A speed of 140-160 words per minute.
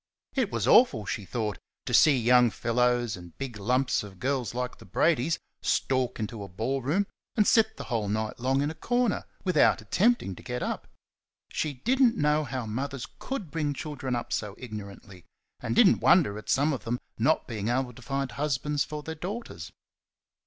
No: average, 190 wpm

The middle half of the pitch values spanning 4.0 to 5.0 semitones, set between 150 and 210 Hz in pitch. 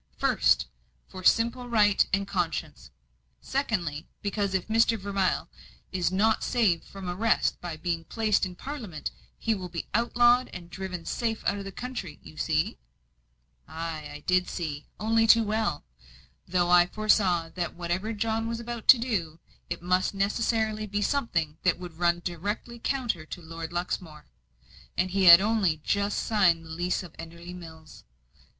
Yes: average, 4.3 semitones; high, 190 Hz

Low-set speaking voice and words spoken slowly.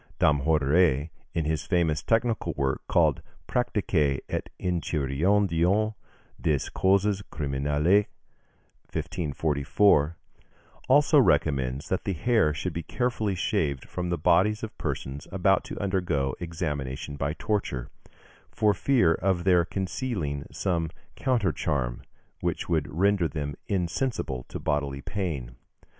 Yes: very low, 85 Hz; slow, 115 wpm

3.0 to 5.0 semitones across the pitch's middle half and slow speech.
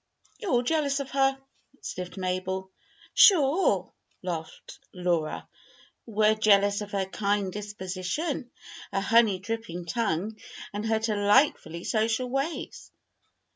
Yes: average, 4.5 semitones; slow, 110 wpm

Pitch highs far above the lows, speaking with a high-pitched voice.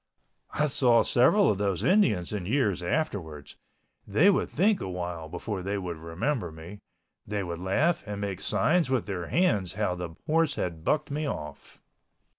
No: wide, 8.2 semitones; low, 100 Hz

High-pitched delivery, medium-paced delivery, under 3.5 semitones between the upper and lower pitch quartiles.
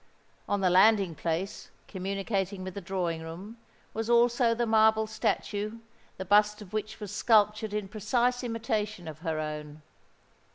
Yes: high, 205 Hz; average, 150 wpm; average, 3.1 semitones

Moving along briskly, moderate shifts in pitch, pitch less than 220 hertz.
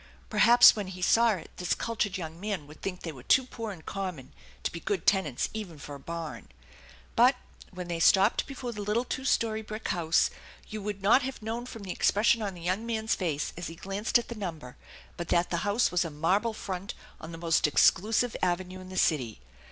Yes: fast, 215 wpm; average, 4.6 semitones; high, 190 Hz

